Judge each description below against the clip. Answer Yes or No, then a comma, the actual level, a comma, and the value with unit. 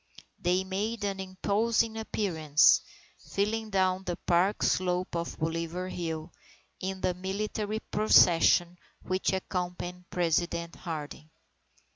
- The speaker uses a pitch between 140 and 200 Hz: Yes, medium, 185 Hz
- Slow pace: Yes, slow, 105 wpm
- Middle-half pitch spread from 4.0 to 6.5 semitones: No, average, 2.7 semitones